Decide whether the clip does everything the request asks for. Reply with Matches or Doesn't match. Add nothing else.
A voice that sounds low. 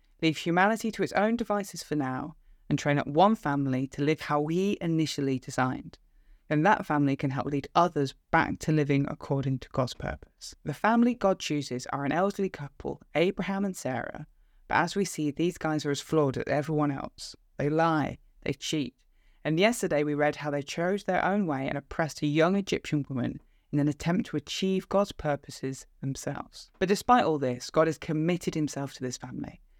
Doesn't match